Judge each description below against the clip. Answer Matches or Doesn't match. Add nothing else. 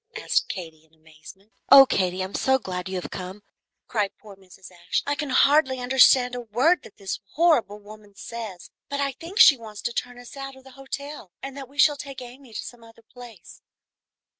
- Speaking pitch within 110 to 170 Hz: Doesn't match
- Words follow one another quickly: Matches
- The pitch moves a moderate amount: Doesn't match